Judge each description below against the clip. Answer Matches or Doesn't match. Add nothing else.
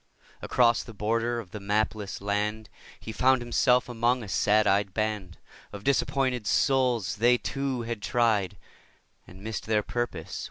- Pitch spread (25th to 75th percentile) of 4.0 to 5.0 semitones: Doesn't match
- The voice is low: Matches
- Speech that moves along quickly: Doesn't match